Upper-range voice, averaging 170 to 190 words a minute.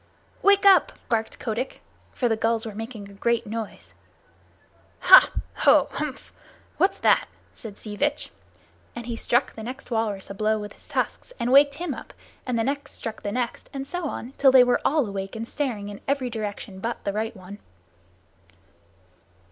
Yes: high, 230 Hz; average, 180 wpm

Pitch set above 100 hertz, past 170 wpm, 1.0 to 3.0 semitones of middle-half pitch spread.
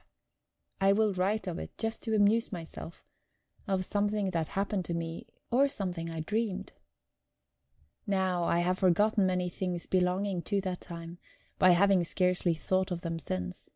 No: medium, 185 Hz; average, 155 wpm; average, 2.7 semitones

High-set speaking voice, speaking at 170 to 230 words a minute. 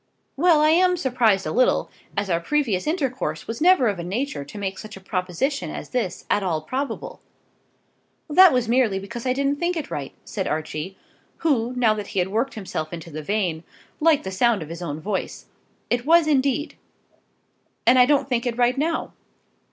Yes: high, 235 Hz; average, 190 wpm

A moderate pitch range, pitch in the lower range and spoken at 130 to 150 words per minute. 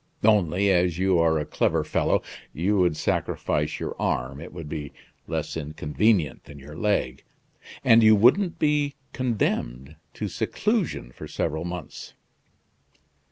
No: wide, 6.4 semitones; very low, 90 Hz; slow, 135 wpm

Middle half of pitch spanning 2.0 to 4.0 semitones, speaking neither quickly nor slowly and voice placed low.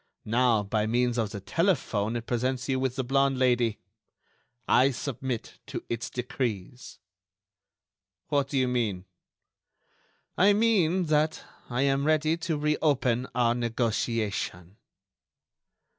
No: average, 3.4 semitones; slow, 125 wpm; low, 125 Hz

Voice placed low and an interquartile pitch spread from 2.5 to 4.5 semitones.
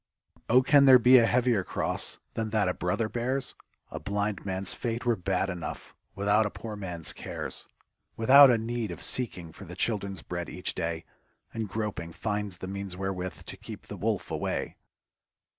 Yes: low, 105 Hz; average, 3.9 semitones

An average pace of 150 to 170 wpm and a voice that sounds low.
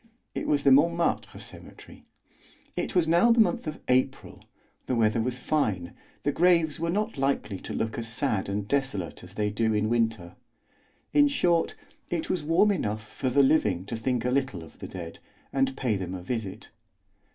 No: average, 185 wpm; low, 125 Hz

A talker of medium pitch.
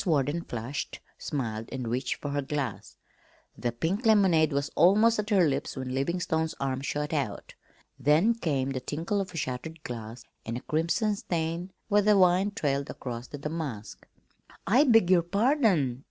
Yes: medium, 155 Hz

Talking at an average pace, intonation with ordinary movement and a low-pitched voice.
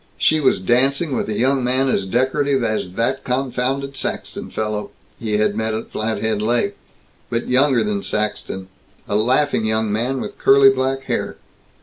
Yes: average, 160 wpm; average, 3.6 semitones; low, 125 Hz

